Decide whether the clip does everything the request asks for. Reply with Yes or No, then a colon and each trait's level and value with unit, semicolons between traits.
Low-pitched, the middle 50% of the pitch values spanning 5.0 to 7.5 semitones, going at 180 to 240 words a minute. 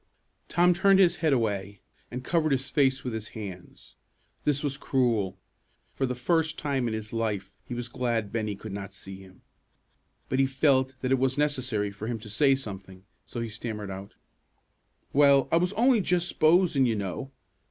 Yes: low, 125 Hz; wide, 5.4 semitones; average, 185 wpm